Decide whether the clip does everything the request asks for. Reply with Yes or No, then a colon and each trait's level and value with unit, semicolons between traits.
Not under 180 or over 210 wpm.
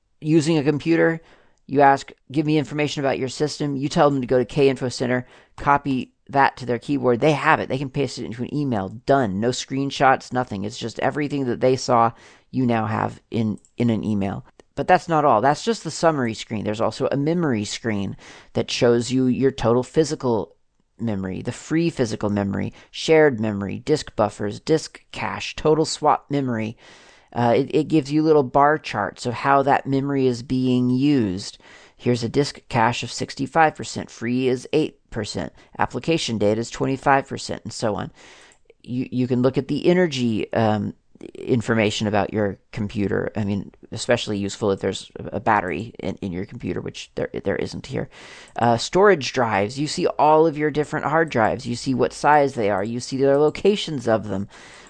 Yes: average, 185 wpm